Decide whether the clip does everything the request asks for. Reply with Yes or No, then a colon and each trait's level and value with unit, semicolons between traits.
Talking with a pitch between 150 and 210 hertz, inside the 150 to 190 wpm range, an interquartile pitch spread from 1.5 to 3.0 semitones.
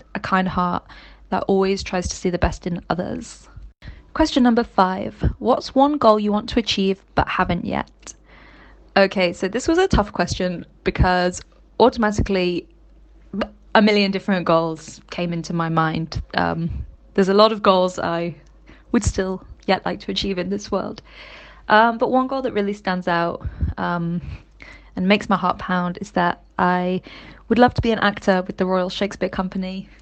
Yes: high, 190 Hz; average, 170 wpm; average, 2.7 semitones